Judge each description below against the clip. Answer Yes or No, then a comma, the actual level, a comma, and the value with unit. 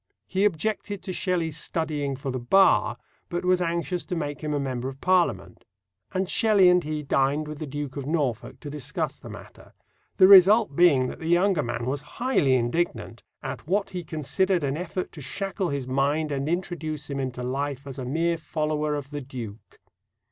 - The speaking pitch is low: No, medium, 150 Hz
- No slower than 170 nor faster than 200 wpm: Yes, average, 190 wpm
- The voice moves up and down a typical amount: Yes, average, 4.6 semitones